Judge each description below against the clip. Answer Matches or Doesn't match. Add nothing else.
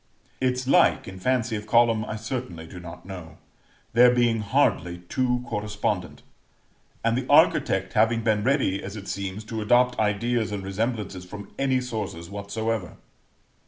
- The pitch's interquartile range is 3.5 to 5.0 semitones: Matches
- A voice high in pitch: Doesn't match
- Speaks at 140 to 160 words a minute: Matches